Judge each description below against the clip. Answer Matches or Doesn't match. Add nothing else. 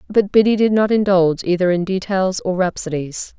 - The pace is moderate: Matches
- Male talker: Doesn't match